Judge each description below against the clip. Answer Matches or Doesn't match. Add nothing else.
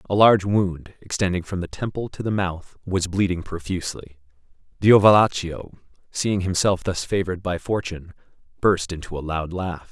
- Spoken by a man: Matches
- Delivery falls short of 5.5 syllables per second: Matches